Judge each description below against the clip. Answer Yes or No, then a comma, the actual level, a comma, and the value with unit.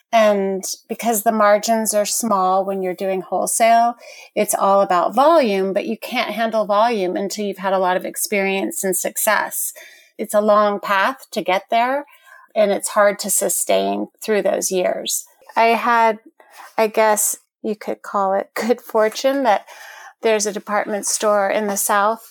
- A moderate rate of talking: Yes, average, 165 wpm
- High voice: Yes, high, 210 Hz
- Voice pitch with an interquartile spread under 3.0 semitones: Yes, narrow, 2.4 semitones